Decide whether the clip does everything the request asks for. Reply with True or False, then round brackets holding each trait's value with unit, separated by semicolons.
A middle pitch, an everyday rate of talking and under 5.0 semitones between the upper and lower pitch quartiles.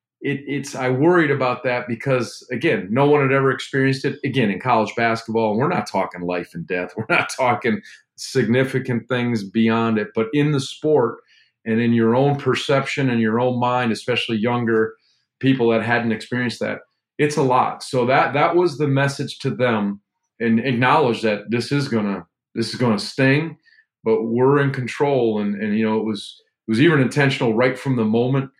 False (125 Hz; 190 wpm; 3.3 semitones)